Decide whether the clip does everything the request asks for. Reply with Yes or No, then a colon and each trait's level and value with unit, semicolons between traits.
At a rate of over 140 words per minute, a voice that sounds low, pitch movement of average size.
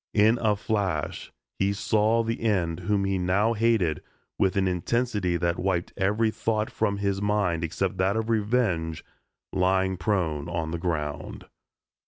Yes: average, 150 wpm; very low, 95 Hz; average, 3.6 semitones